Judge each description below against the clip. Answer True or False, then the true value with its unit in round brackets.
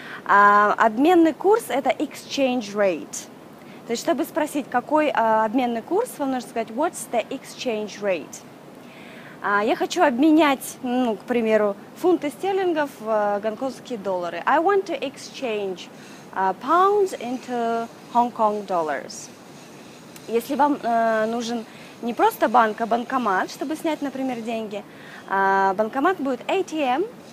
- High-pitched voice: True (245 Hz)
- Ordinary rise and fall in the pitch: False (5.9 semitones)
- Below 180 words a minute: True (120 wpm)